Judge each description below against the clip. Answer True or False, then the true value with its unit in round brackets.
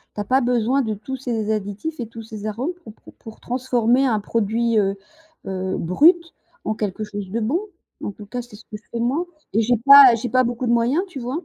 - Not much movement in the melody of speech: False (3.2 semitones)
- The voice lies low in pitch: False (230 Hz)